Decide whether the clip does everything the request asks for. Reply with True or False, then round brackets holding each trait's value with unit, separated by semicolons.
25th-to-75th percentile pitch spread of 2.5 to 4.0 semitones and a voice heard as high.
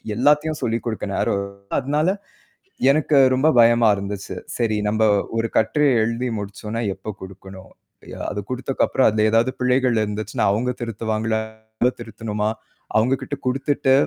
False (3.1 semitones; 115 Hz)